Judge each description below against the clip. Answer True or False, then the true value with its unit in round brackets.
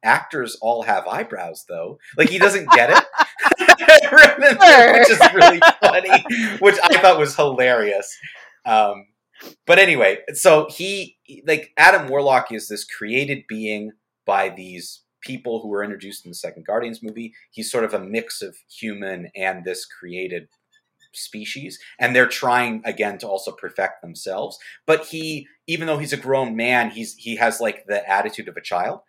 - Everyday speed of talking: True (160 wpm)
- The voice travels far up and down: True (7.9 semitones)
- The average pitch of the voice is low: True (120 Hz)